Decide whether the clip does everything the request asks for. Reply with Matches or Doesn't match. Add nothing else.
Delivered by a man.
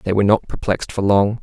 Matches